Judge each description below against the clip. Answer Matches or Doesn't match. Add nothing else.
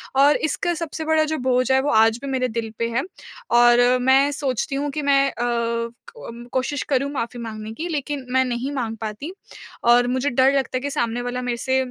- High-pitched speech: Matches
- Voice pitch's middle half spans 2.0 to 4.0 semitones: Matches